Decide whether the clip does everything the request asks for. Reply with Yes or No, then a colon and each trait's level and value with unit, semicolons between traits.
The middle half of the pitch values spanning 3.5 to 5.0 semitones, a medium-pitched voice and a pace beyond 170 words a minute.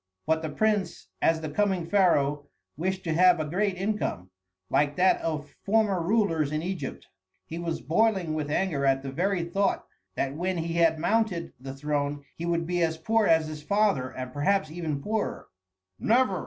Yes: average, 4.3 semitones; medium, 165 Hz; average, 180 wpm